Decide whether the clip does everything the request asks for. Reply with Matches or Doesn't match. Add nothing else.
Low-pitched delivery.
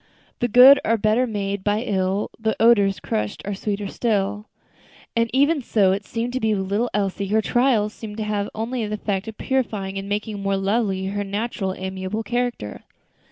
Doesn't match